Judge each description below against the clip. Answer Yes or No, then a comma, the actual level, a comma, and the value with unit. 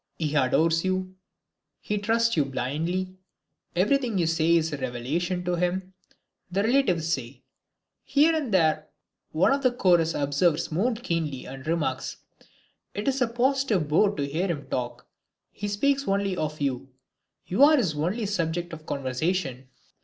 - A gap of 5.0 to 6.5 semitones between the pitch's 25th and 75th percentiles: Yes, average, 5.3 semitones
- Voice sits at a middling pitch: Yes, medium, 175 Hz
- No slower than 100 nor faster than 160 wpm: Yes, average, 155 wpm